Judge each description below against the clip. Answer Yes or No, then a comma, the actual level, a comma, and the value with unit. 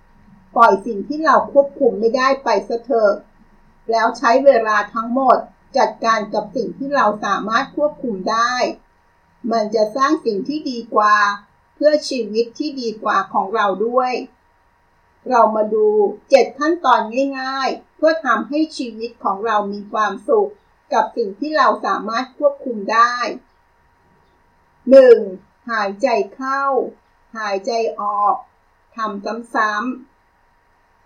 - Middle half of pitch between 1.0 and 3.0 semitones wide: No, average, 4.3 semitones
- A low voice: No, high, 230 Hz